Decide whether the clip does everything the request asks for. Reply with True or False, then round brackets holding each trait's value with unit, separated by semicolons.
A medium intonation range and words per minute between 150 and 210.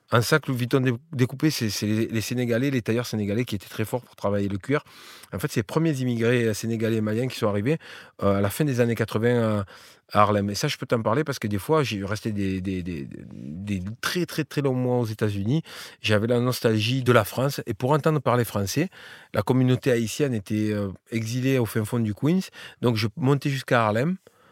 False (4.1 semitones; 220 wpm)